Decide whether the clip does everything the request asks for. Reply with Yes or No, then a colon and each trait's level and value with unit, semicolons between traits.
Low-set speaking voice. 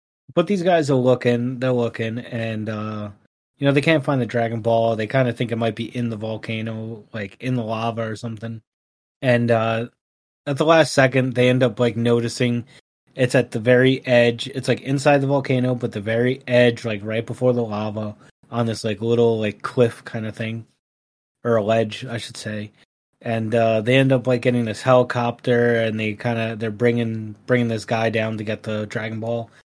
Yes: low, 115 Hz